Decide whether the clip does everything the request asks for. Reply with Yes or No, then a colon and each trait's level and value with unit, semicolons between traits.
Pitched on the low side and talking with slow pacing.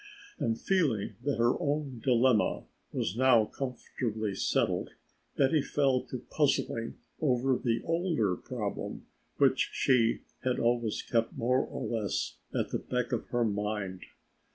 Yes: low, 120 Hz; slow, 130 wpm